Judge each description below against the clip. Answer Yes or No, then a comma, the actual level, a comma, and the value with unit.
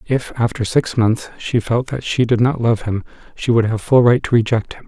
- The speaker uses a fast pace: Yes, fast, 245 wpm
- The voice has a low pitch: Yes, low, 120 Hz